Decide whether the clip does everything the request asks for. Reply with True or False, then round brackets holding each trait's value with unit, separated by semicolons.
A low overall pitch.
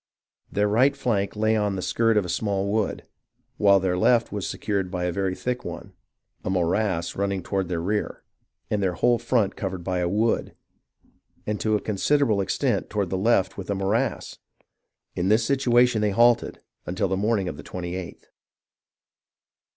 True (100 Hz)